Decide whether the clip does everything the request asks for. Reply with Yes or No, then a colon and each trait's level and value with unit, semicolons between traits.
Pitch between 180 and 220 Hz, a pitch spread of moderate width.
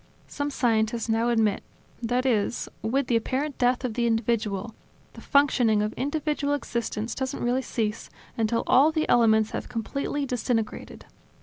No: high, 235 Hz; average, 3.0 semitones